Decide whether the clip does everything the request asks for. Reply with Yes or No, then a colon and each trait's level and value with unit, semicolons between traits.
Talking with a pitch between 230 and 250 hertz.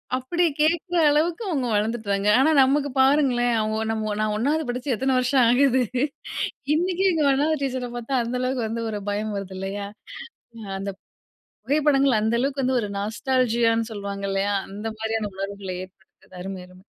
Yes: high, 240 Hz